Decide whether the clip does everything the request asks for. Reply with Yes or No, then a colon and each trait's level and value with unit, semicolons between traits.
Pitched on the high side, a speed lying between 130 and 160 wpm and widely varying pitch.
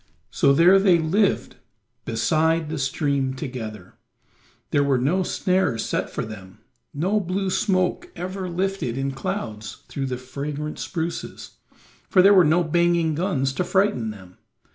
No: medium, 155 Hz; average, 140 wpm; wide, 5.7 semitones